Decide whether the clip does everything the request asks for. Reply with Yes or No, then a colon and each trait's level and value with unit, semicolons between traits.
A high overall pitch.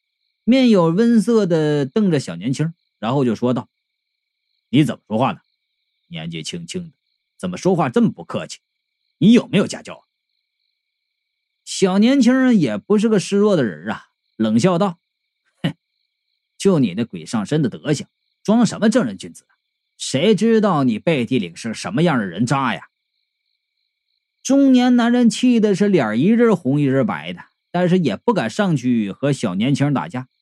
Yes: high, 225 Hz